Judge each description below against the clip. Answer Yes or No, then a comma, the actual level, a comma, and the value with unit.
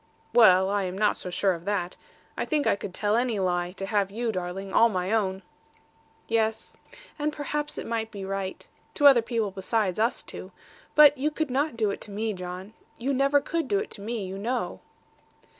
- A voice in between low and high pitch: No, high, 215 Hz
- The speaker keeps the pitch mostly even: No, average, 4.3 semitones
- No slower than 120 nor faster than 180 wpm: No, fast, 205 wpm